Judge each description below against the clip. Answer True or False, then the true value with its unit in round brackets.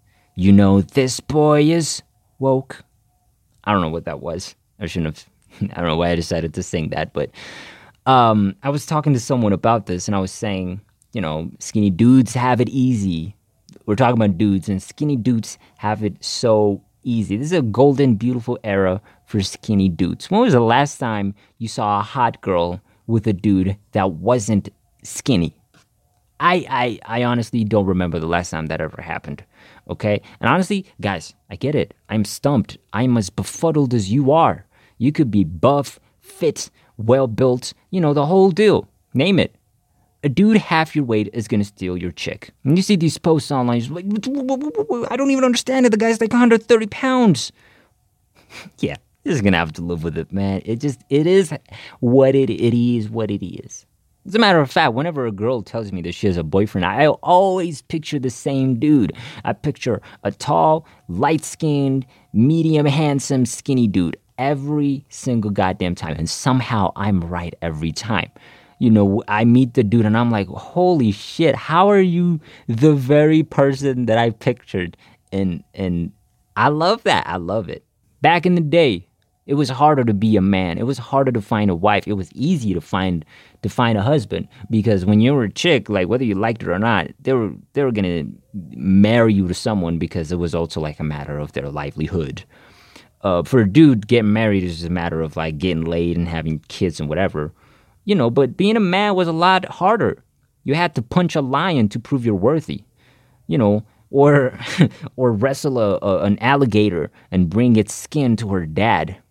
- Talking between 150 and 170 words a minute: False (195 wpm)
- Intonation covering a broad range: True (6.1 semitones)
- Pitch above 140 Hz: False (115 Hz)